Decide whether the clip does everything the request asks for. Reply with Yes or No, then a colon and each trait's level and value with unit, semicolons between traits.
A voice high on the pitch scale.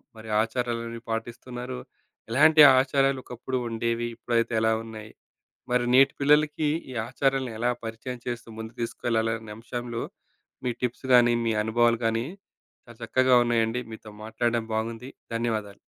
No: low, 120 Hz